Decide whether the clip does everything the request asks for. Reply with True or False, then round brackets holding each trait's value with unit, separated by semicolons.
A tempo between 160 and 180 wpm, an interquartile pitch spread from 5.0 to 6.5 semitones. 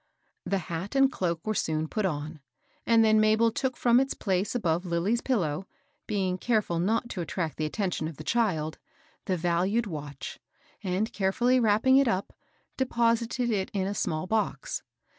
True (170 wpm; 5.3 semitones)